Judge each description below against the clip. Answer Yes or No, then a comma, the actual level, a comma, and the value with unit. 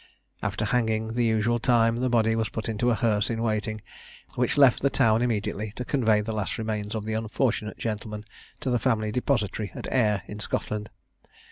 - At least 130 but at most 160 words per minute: No, average, 190 wpm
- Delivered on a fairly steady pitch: Yes, narrow, 1.9 semitones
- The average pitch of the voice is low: Yes, low, 110 Hz